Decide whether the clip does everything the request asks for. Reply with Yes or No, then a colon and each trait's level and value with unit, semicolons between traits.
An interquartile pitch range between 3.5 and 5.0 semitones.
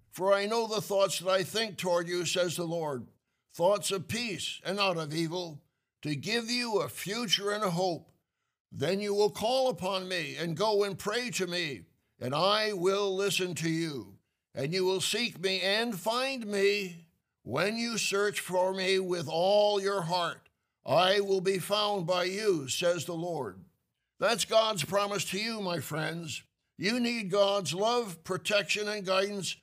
No: average, 2.8 semitones